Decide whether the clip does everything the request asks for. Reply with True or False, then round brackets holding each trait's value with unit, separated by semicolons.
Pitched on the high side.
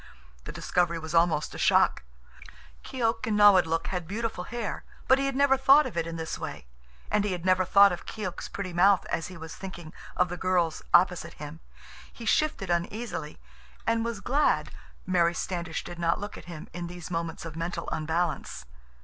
False (180 Hz)